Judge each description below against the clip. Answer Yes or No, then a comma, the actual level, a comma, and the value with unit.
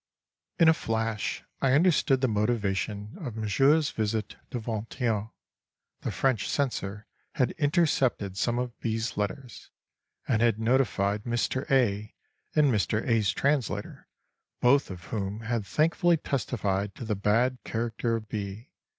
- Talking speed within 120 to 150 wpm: Yes, average, 140 wpm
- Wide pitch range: No, average, 3.9 semitones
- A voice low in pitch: Yes, low, 115 Hz